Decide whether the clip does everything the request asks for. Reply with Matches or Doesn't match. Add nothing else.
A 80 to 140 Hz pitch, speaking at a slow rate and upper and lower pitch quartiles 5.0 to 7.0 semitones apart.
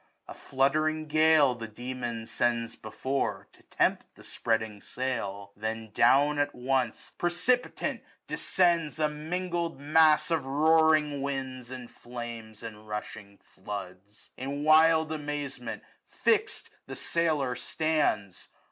Matches